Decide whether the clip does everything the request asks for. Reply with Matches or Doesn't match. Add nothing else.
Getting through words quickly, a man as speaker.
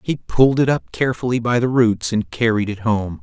Matches